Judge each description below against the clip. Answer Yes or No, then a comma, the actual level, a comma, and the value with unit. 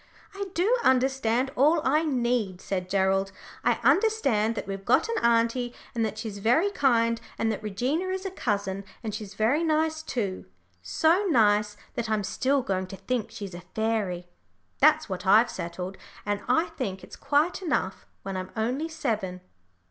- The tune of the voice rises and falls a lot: Yes, wide, 6.3 semitones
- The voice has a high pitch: Yes, high, 230 Hz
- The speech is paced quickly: No, average, 170 wpm